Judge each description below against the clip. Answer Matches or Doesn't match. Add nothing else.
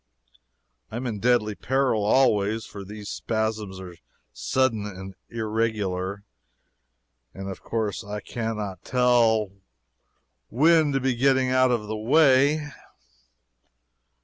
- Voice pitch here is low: Matches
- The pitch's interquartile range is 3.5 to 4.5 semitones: Matches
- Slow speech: Matches